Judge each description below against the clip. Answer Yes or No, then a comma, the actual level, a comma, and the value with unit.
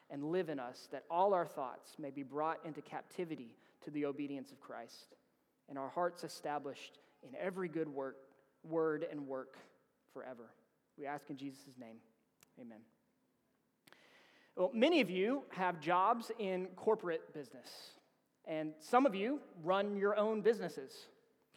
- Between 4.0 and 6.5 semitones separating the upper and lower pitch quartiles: Yes, average, 4.9 semitones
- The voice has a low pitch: No, medium, 160 Hz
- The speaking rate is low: No, average, 145 wpm